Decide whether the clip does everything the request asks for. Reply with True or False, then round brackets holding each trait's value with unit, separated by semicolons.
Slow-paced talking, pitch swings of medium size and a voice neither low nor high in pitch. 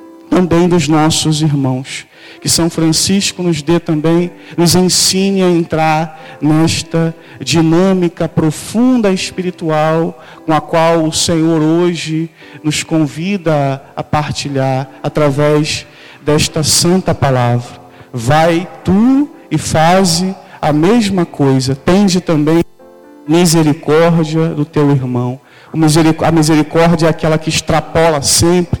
False (110 wpm; 2.3 semitones; 160 Hz)